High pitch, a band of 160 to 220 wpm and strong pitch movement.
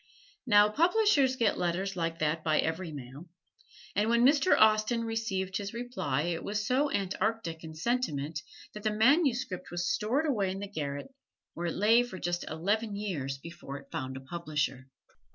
Yes: high, 195 Hz; average, 170 wpm; wide, 6.1 semitones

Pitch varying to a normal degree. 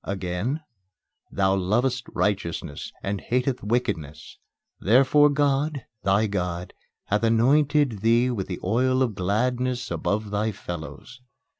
Yes: average, 4.8 semitones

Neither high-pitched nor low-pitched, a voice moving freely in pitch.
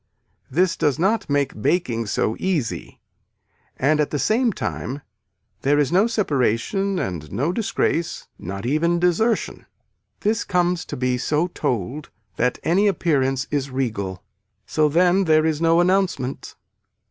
Yes: medium, 150 Hz; wide, 5.8 semitones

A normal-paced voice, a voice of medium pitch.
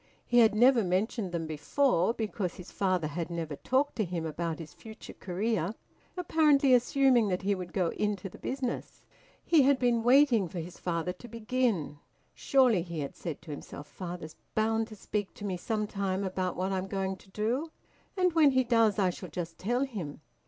No: average, 190 wpm; high, 200 Hz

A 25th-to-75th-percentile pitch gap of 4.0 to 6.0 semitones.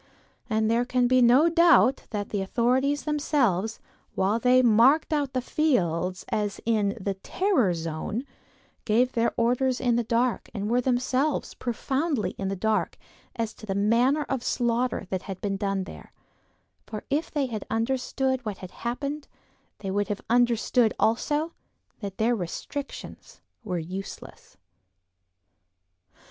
Yes: average, 4.3 semitones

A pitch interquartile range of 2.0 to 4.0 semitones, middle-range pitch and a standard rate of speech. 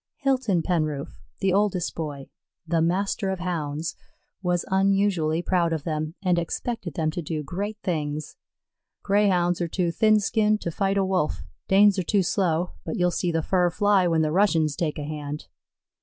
Yes: average, 3.6 semitones; medium, 175 Hz; average, 170 wpm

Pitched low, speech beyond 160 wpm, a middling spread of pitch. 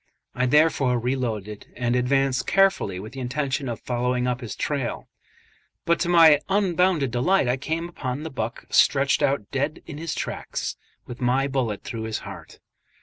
Yes: low, 130 Hz; average, 170 wpm; average, 3.7 semitones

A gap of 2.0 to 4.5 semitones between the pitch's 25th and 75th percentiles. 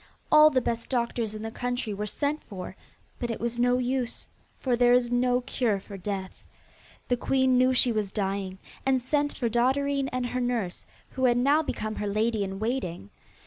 Yes: average, 3.2 semitones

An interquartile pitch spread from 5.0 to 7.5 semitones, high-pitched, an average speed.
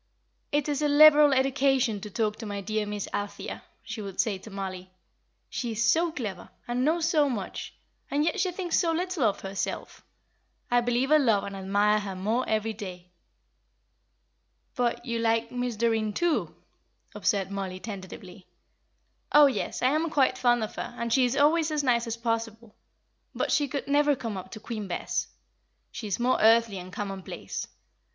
Yes: wide, 5.4 semitones; high, 230 Hz; average, 175 wpm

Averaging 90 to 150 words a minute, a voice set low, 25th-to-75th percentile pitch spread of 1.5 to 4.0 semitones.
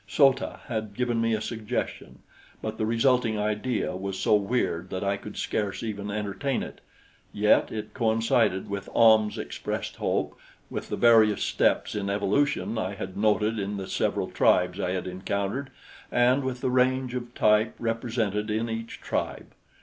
No: average, 165 wpm; low, 110 Hz; average, 2.9 semitones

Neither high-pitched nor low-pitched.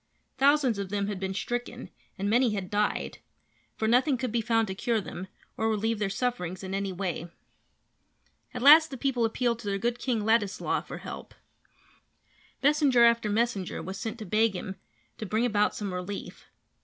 No: high, 220 Hz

